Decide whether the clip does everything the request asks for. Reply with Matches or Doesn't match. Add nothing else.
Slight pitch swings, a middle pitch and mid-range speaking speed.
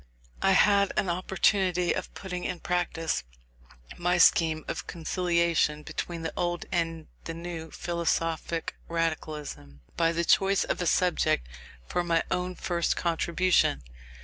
Doesn't match